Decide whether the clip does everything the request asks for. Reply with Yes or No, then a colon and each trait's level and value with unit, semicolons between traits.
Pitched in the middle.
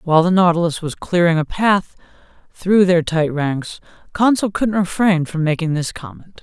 Yes: medium, 175 Hz